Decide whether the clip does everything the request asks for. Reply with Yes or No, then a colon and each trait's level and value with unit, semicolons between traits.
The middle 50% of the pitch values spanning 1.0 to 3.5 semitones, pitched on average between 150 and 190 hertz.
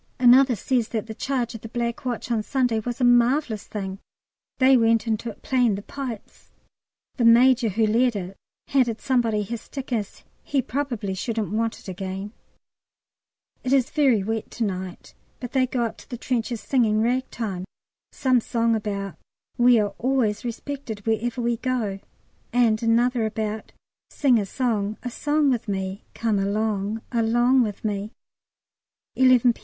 No: average, 2.8 semitones; high, 230 Hz